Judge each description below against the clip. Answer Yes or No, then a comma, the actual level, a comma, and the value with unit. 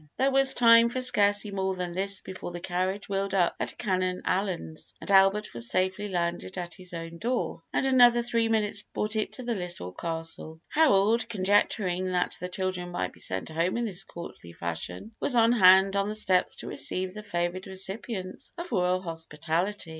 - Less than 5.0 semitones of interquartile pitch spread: Yes, average, 3.1 semitones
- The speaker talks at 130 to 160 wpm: No, average, 185 wpm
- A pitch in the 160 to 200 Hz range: Yes, high, 190 Hz